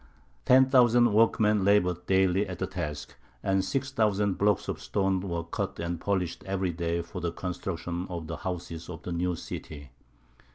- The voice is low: Yes, very low, 90 Hz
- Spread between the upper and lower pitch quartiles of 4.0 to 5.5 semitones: No, average, 3.1 semitones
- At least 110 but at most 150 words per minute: No, average, 170 wpm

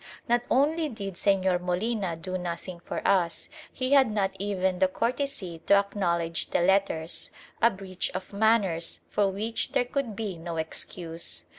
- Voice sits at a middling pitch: No, high, 195 Hz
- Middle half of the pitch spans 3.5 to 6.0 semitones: Yes, average, 4.0 semitones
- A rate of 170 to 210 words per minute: No, average, 155 wpm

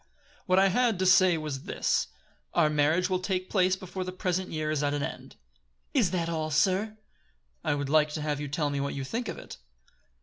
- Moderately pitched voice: Yes, medium, 170 Hz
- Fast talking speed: Yes, fast, 215 wpm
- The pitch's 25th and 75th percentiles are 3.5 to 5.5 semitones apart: Yes, average, 3.8 semitones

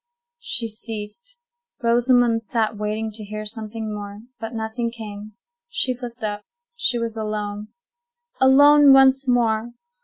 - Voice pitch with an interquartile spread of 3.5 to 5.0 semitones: No, narrow, 2.5 semitones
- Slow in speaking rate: Yes, slow, 125 wpm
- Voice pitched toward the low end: No, high, 225 Hz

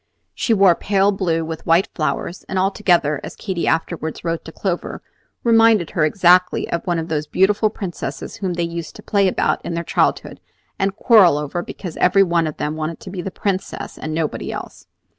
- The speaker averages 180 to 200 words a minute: Yes, average, 195 wpm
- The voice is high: No, medium, 175 Hz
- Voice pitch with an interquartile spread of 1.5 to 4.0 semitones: Yes, average, 3.0 semitones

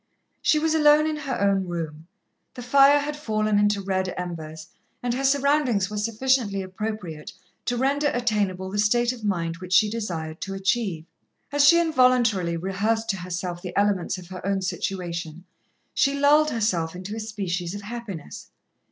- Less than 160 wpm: No, average, 165 wpm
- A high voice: Yes, high, 205 Hz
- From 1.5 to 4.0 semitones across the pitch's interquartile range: No, average, 5.3 semitones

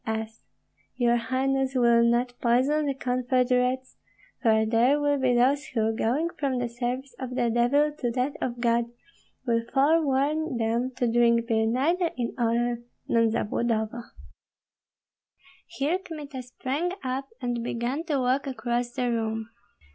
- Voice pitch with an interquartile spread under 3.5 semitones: Yes, narrow, 2.5 semitones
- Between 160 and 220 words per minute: No, average, 145 wpm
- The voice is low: No, very high, 250 Hz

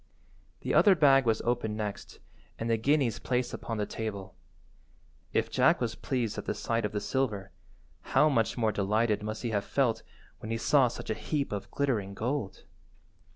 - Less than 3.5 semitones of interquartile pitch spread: No, average, 3.8 semitones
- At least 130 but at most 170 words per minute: No, average, 180 wpm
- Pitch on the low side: Yes, low, 115 Hz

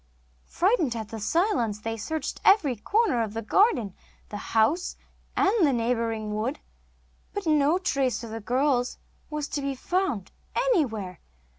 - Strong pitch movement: Yes, wide, 7.0 semitones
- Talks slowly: No, average, 145 wpm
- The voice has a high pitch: Yes, very high, 255 Hz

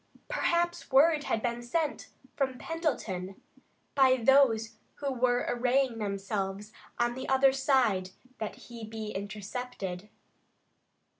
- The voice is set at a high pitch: Yes, high, 240 Hz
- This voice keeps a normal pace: No, slow, 115 wpm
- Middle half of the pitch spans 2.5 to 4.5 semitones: Yes, average, 4.2 semitones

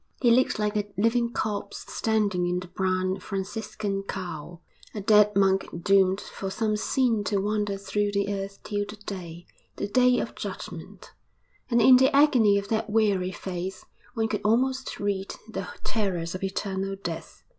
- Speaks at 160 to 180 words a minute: Yes, average, 165 wpm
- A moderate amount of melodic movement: No, narrow, 2.3 semitones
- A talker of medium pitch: No, high, 200 Hz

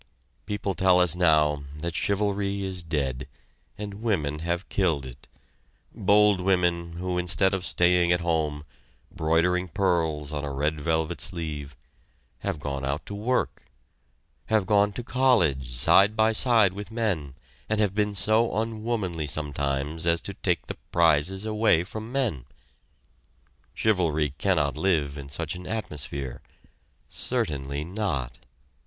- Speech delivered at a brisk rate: No, slow, 135 wpm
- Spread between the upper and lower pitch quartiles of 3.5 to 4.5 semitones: No, average, 5.3 semitones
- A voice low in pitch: Yes, very low, 85 Hz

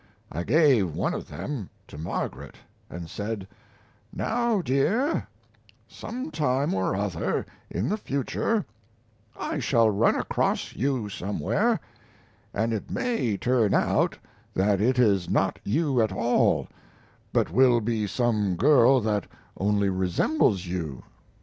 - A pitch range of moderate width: No, wide, 5.8 semitones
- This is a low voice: Yes, low, 110 Hz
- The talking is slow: Yes, slow, 125 wpm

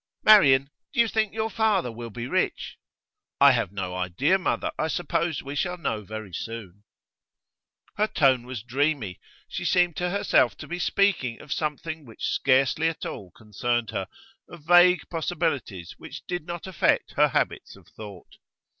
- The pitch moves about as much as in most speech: No, wide, 7.6 semitones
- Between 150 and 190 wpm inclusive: Yes, average, 165 wpm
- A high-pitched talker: No, medium, 140 Hz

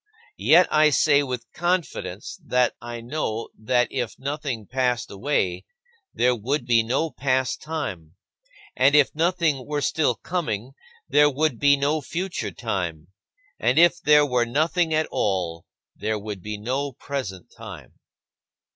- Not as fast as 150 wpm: Yes, average, 140 wpm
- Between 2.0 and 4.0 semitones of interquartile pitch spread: No, average, 4.9 semitones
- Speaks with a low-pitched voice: Yes, low, 130 Hz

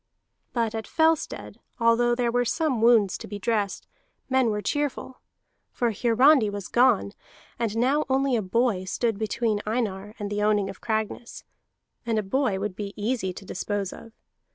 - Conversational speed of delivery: Yes, average, 165 wpm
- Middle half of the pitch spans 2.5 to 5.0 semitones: Yes, average, 3.0 semitones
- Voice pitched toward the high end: Yes, high, 225 Hz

